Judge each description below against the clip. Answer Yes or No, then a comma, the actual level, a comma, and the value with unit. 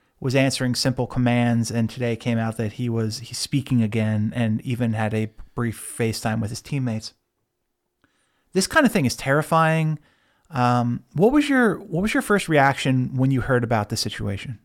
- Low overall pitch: Yes, low, 120 Hz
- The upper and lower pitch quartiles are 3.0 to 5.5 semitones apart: Yes, average, 3.5 semitones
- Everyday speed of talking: Yes, average, 180 wpm